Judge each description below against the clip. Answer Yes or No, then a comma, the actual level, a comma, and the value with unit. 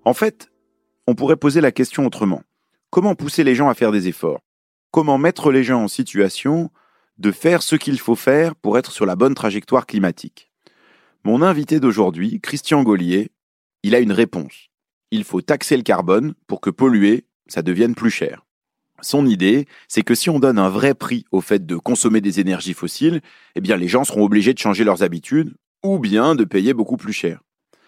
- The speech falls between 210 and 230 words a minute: No, average, 195 wpm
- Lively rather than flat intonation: Yes, wide, 7.2 semitones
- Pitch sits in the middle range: No, low, 125 Hz